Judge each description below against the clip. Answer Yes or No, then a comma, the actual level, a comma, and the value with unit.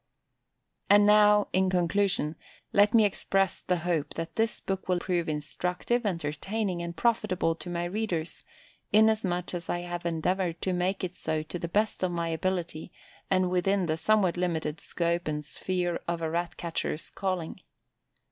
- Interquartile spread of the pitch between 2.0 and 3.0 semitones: Yes, narrow, 2.5 semitones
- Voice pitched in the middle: Yes, medium, 180 Hz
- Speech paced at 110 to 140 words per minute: No, average, 160 wpm